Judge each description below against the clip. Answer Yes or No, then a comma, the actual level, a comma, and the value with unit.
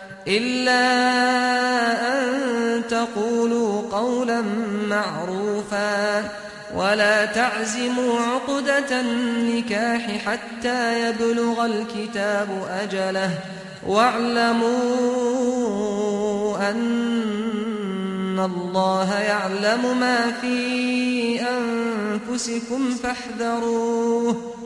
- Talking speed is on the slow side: Yes, slow, 50 wpm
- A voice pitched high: Yes, high, 230 Hz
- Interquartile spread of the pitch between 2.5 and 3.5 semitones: Yes, average, 2.8 semitones